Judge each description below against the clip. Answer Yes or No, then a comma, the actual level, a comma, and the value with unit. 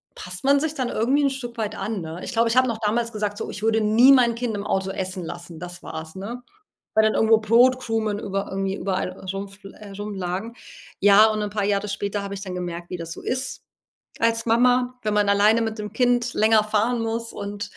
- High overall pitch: Yes, high, 215 Hz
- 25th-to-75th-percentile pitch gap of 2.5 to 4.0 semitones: Yes, average, 2.8 semitones